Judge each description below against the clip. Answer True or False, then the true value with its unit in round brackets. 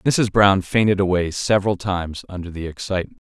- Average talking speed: True (165 wpm)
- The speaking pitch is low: True (95 Hz)